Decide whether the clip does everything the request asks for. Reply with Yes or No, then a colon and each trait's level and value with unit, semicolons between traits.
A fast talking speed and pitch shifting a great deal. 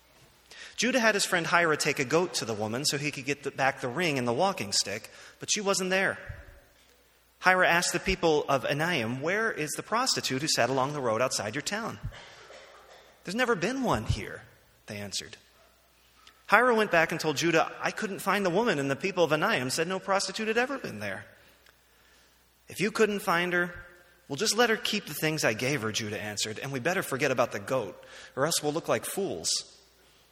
Yes: fast, 210 wpm; wide, 5.8 semitones